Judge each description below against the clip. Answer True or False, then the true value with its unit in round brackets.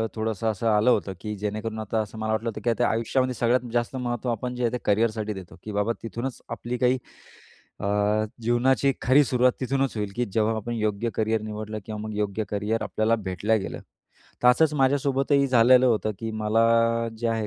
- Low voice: True (115 Hz)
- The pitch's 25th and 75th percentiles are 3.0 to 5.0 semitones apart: False (2.4 semitones)